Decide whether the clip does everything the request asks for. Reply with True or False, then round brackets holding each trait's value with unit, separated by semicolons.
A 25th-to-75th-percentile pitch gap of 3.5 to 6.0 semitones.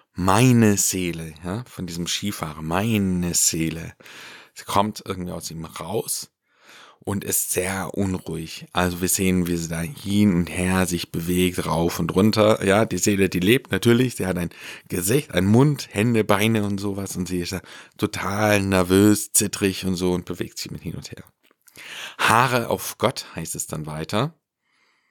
False (2.9 semitones)